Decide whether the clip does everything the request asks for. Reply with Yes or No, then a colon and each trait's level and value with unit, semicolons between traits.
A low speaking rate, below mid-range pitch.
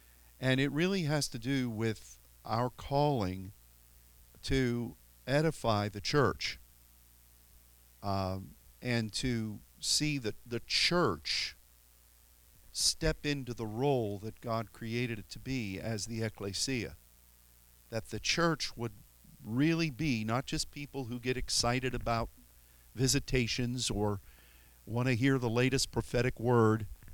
Yes: slow, 120 wpm; low, 115 Hz